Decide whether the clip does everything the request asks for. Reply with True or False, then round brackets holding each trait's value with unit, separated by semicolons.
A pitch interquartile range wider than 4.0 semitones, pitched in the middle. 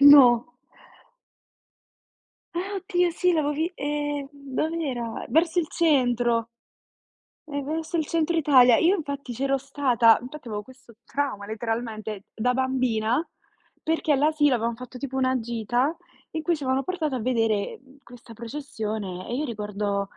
False (4.5 semitones; 265 Hz)